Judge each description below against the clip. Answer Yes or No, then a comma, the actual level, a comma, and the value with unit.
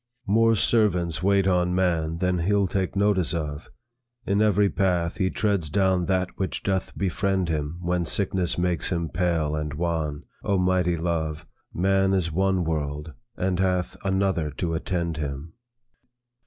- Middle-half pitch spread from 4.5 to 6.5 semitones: No, average, 2.7 semitones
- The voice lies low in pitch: Yes, very low, 90 Hz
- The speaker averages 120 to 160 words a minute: Yes, average, 150 wpm